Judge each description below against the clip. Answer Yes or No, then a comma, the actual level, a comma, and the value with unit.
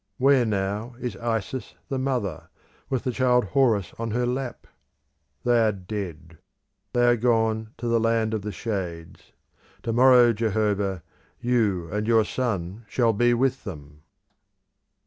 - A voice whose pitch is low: Yes, low, 115 Hz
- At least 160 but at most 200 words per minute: No, average, 145 wpm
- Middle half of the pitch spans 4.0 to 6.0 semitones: No, average, 3.3 semitones